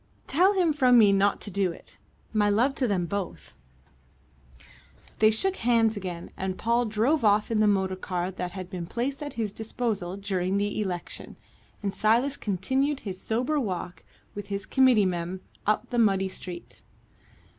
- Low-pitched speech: No, high, 205 Hz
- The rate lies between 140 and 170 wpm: Yes, average, 165 wpm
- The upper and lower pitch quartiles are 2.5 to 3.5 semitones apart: No, average, 4.3 semitones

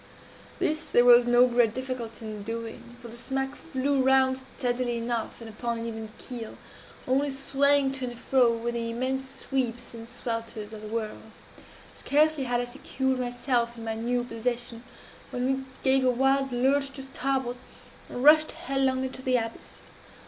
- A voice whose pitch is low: No, high, 245 Hz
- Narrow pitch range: Yes, narrow, 2.3 semitones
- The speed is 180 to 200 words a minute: No, average, 170 wpm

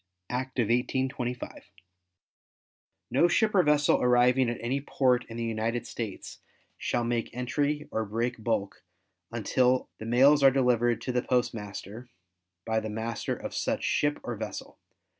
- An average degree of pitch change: No, narrow, 2.3 semitones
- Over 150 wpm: No, average, 145 wpm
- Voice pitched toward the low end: Yes, low, 120 Hz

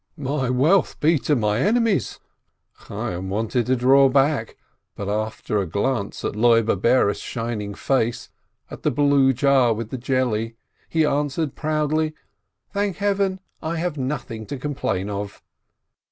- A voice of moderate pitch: No, low, 130 Hz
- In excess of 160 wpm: No, average, 140 wpm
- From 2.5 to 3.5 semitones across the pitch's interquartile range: No, average, 5.2 semitones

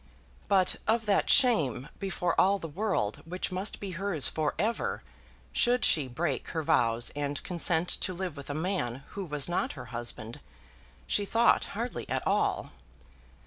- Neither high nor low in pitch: Yes, medium, 175 Hz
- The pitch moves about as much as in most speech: No, wide, 5.8 semitones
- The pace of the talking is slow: No, average, 160 wpm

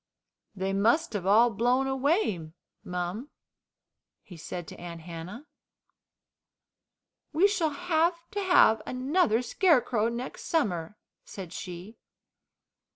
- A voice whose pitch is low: No, high, 230 Hz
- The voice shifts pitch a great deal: Yes, wide, 8.7 semitones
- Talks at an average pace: No, slow, 105 wpm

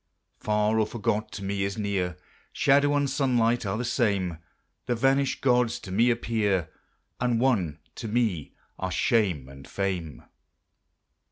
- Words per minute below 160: Yes, average, 145 wpm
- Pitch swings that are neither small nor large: Yes, average, 4.3 semitones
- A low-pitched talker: Yes, low, 110 Hz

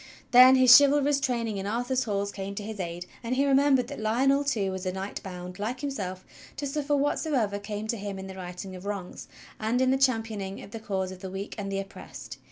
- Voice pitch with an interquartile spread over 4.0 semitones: Yes, average, 5.2 semitones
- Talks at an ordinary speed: No, fast, 230 wpm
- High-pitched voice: Yes, high, 215 Hz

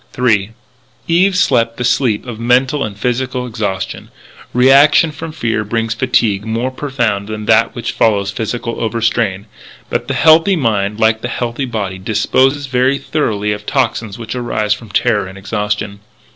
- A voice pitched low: Yes, low, 115 Hz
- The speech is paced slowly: No, average, 160 wpm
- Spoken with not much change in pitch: No, average, 3.4 semitones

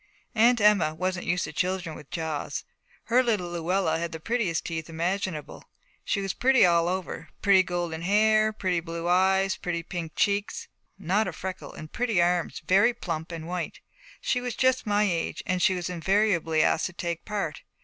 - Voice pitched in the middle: Yes, medium, 180 Hz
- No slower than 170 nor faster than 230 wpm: Yes, average, 180 wpm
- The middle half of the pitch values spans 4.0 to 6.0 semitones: No, average, 3.4 semitones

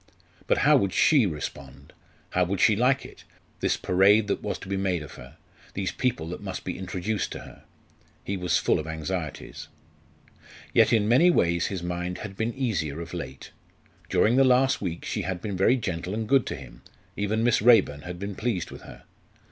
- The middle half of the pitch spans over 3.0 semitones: Yes, average, 4.3 semitones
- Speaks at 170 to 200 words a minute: Yes, average, 195 wpm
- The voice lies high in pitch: No, very low, 95 Hz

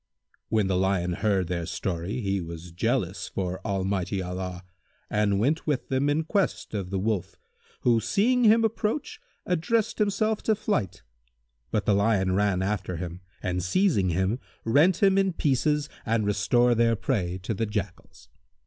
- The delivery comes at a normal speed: Yes, average, 160 wpm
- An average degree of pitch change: No, wide, 7.8 semitones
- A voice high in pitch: No, low, 105 Hz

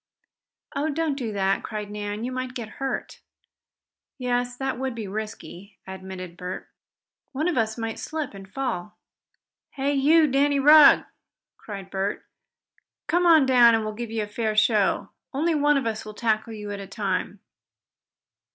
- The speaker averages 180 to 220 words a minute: No, average, 160 wpm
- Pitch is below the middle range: No, high, 225 Hz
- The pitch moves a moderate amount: Yes, average, 4.8 semitones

